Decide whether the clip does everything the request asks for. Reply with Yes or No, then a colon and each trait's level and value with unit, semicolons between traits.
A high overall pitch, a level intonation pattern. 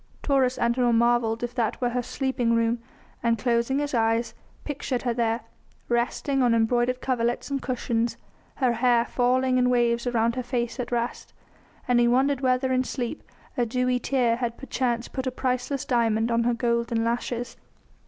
Yes: high, 240 Hz; narrow, 1.4 semitones